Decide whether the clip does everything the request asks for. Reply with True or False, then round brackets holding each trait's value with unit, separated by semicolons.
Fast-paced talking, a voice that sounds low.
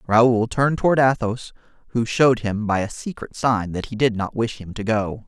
True (215 wpm; 115 Hz)